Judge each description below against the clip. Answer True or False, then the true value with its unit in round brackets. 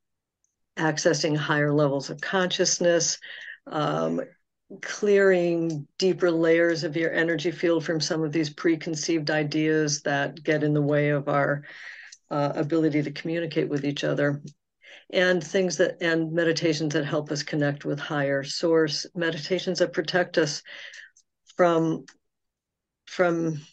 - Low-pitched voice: False (165 Hz)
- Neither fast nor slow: False (130 wpm)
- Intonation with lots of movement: False (2.5 semitones)